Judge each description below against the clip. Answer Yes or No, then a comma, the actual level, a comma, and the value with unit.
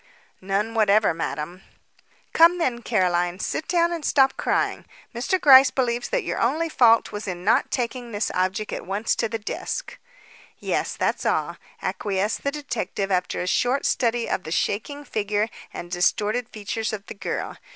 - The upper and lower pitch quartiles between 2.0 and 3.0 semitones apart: No, average, 4.6 semitones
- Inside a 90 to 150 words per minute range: No, average, 165 wpm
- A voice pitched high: Yes, high, 220 Hz